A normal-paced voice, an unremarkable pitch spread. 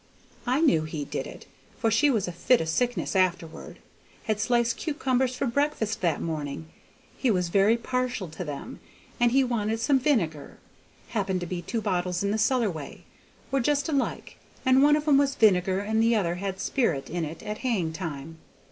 No: average, 190 wpm; wide, 6.4 semitones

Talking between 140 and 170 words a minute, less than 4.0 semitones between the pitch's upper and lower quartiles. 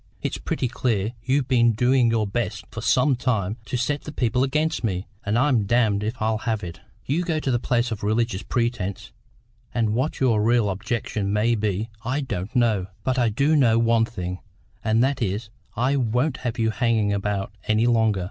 No: average, 195 wpm; average, 3.1 semitones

